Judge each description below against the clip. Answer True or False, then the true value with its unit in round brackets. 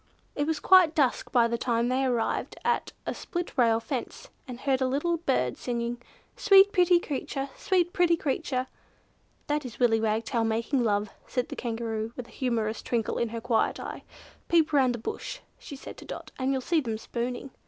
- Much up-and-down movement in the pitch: False (4.3 semitones)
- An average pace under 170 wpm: False (190 wpm)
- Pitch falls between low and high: False (255 Hz)